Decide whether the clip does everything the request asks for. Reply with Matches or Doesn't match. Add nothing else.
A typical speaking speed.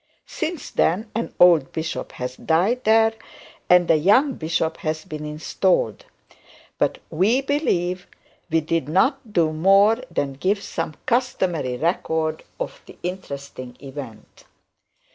Doesn't match